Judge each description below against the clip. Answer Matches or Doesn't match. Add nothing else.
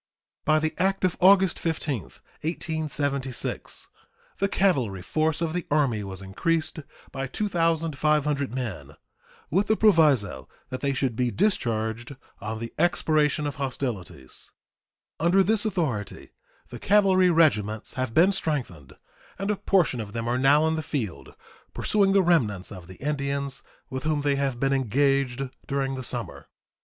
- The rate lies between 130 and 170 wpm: Matches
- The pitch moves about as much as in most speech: Doesn't match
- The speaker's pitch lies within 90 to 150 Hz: Matches